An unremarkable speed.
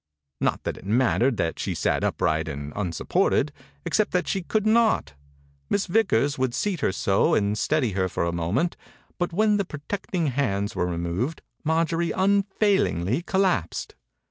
Yes: average, 155 wpm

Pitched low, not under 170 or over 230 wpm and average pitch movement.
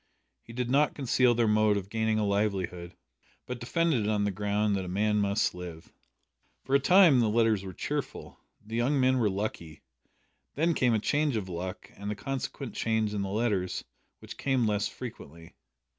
Yes: low, 110 Hz; average, 190 wpm; average, 3.8 semitones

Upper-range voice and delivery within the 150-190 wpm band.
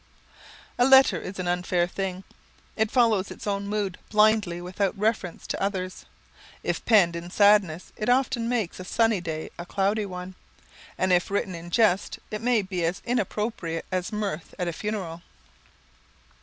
Yes: high, 195 Hz; average, 160 wpm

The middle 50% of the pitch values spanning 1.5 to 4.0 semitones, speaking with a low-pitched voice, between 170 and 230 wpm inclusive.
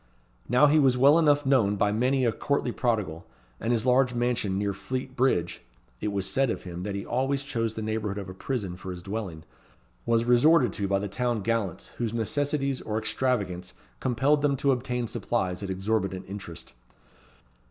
No: average, 4.8 semitones; low, 115 Hz; average, 185 wpm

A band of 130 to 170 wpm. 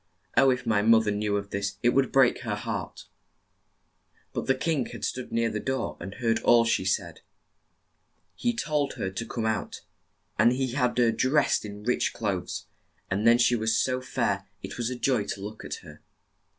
No: average, 195 wpm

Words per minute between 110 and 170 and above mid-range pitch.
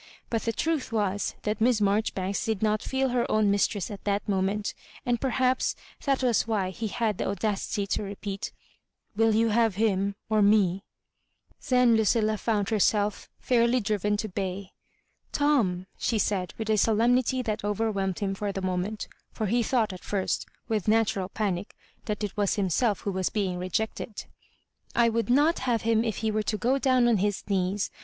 No: average, 195 wpm; high, 215 Hz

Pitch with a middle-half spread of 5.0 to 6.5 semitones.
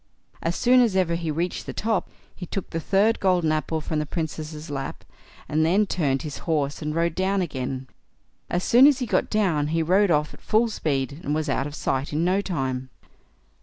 No: average, 4.3 semitones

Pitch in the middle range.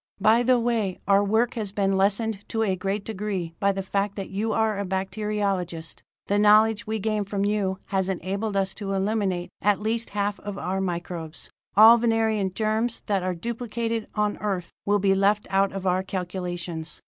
No: high, 200 Hz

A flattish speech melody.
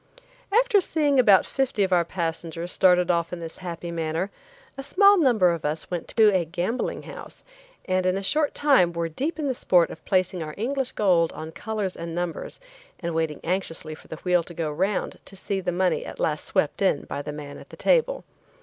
No: average, 4.8 semitones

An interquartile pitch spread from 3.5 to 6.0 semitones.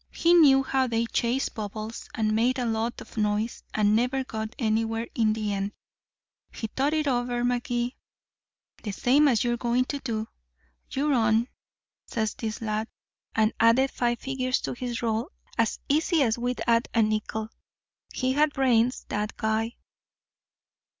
No: average, 2.7 semitones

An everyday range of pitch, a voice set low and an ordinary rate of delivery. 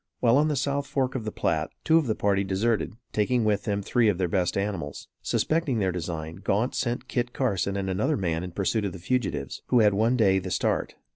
No: average, 4.6 semitones; low, 105 Hz; fast, 225 wpm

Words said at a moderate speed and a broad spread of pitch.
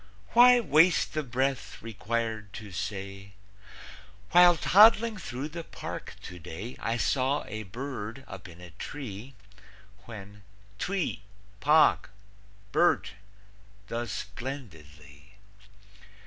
No: slow, 100 wpm; wide, 7.0 semitones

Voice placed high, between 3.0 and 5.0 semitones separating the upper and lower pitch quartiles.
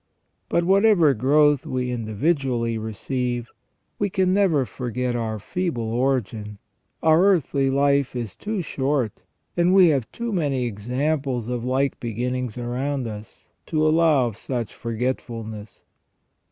No: low, 130 Hz; average, 4.7 semitones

